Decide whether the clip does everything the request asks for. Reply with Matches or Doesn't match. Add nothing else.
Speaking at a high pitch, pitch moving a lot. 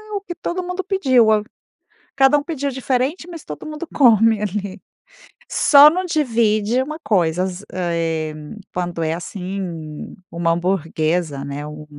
Matches